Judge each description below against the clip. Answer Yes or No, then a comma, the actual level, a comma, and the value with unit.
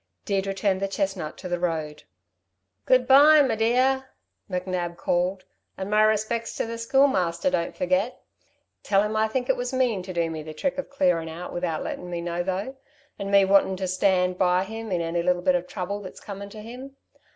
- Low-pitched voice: No, high, 195 Hz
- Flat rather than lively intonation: No, average, 4.1 semitones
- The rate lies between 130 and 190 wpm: No, average, 200 wpm